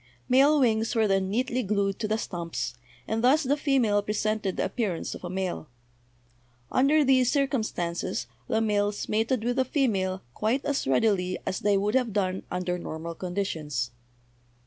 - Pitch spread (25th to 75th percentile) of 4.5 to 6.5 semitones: Yes, average, 5.3 semitones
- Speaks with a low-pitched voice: No, high, 210 Hz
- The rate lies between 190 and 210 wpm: No, average, 170 wpm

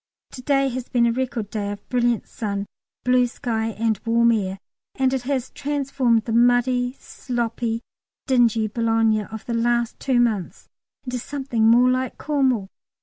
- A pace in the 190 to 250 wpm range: No, average, 155 wpm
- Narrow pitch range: Yes, narrow, 2.1 semitones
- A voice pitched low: No, high, 235 Hz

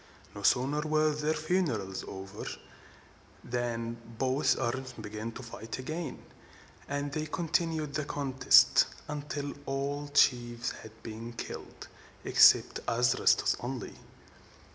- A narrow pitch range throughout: No, average, 4.1 semitones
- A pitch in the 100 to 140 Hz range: Yes, low, 135 Hz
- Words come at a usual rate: No, slow, 115 wpm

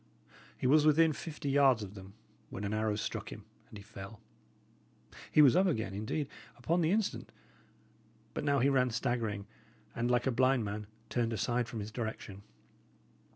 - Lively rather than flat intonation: No, average, 5.0 semitones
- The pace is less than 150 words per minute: No, average, 170 wpm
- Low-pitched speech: Yes, low, 120 Hz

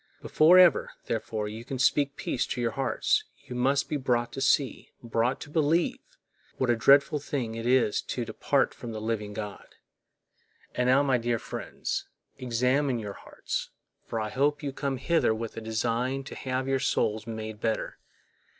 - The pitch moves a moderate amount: Yes, average, 3.3 semitones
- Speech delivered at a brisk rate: No, average, 170 wpm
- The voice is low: Yes, low, 125 Hz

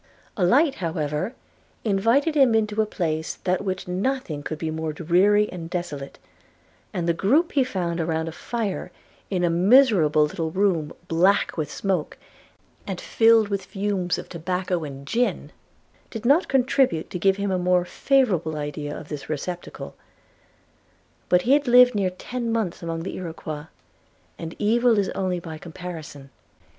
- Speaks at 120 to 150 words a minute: No, average, 160 wpm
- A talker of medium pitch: Yes, medium, 180 Hz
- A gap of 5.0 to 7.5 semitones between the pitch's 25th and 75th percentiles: Yes, average, 5.3 semitones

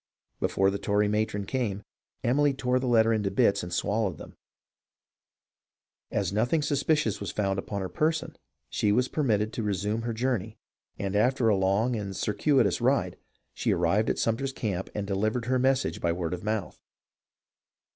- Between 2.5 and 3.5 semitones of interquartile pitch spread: No, average, 4.2 semitones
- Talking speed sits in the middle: Yes, average, 165 wpm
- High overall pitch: No, low, 110 Hz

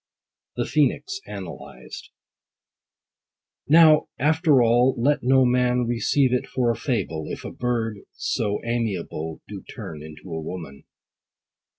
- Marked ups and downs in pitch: Yes, wide, 5.8 semitones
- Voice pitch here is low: Yes, low, 120 Hz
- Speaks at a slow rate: Yes, slow, 120 wpm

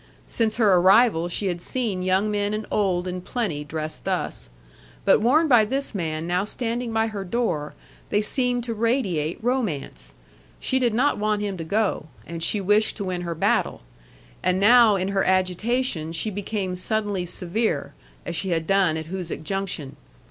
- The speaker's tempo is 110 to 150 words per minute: No, average, 175 wpm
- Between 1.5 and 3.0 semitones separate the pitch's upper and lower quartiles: No, average, 4.1 semitones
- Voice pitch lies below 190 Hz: No, high, 195 Hz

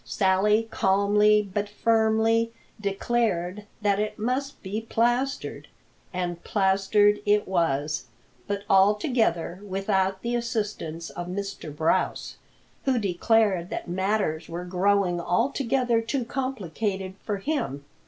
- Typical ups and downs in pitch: Yes, average, 3.3 semitones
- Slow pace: Yes, slow, 110 wpm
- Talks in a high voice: Yes, high, 205 Hz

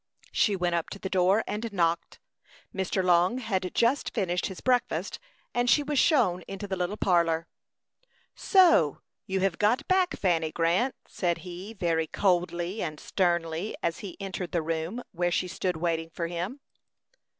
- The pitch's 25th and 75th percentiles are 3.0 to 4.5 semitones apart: Yes, average, 3.5 semitones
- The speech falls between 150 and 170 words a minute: Yes, average, 160 wpm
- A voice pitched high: No, medium, 180 Hz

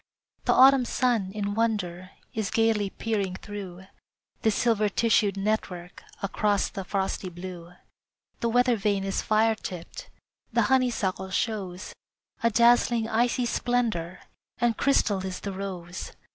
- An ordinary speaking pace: No, slow, 130 wpm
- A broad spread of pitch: No, average, 3.4 semitones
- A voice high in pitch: Yes, high, 205 Hz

